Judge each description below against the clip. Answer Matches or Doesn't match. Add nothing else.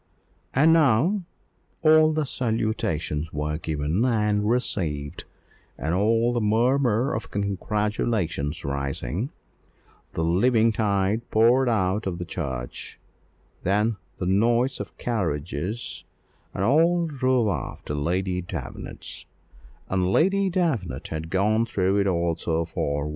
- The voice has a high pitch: Doesn't match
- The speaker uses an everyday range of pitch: Doesn't match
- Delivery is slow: Matches